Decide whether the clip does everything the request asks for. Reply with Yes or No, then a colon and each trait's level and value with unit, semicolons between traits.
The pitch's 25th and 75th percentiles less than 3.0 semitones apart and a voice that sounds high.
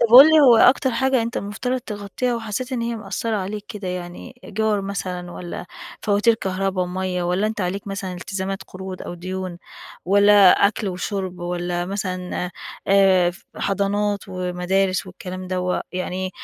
Yes: narrow, 2.5 semitones; high, 195 Hz